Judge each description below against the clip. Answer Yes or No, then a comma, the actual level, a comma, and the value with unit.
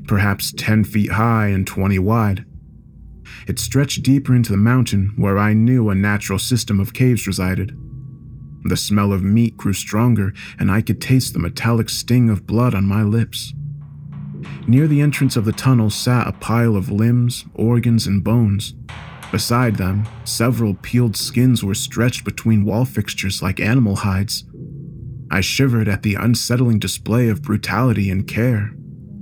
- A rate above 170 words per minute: No, average, 160 wpm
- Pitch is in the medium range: No, low, 115 Hz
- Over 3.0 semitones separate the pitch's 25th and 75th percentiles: Yes, average, 3.6 semitones